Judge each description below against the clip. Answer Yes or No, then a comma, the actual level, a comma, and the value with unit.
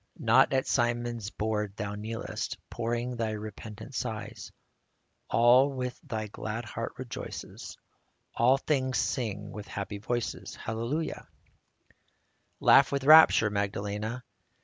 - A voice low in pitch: Yes, low, 115 Hz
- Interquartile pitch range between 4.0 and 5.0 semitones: No, average, 2.9 semitones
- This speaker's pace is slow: Yes, slow, 115 wpm